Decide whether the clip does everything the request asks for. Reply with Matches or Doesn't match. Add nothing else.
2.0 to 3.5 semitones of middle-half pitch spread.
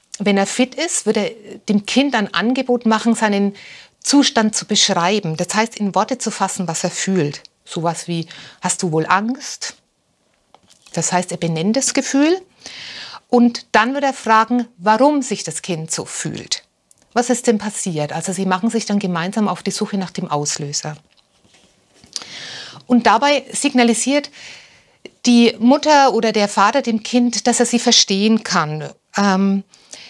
Doesn't match